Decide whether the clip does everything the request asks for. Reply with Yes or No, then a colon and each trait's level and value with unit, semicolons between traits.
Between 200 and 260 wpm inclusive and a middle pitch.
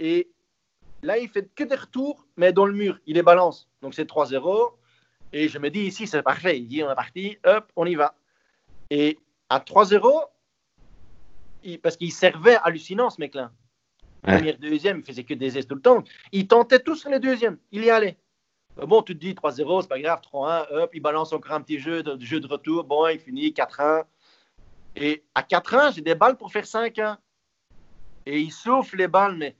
Yes: average, 215 wpm; medium, 170 Hz